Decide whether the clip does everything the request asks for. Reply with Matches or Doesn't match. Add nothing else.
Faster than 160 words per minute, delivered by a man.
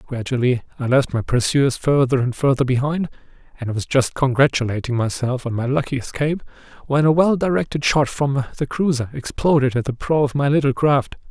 Matches